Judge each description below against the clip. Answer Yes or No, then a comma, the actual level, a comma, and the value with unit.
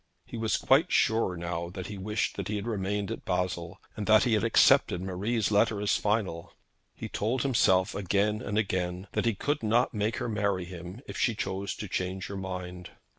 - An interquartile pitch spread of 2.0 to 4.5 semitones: Yes, average, 2.9 semitones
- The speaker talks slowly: No, average, 195 wpm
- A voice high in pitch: No, low, 100 Hz